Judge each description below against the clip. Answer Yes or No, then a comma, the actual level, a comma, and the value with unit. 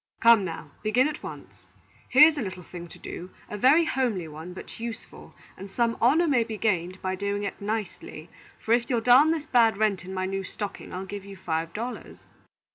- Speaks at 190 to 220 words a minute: Yes, average, 200 wpm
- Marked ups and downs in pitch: No, average, 4.4 semitones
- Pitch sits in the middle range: No, high, 210 Hz